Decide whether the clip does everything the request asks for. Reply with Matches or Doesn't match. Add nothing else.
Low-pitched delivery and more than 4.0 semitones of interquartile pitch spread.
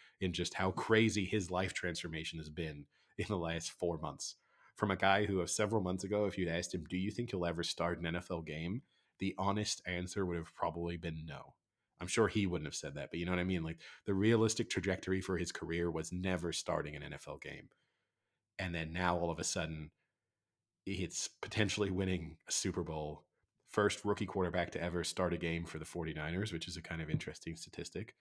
Doesn't match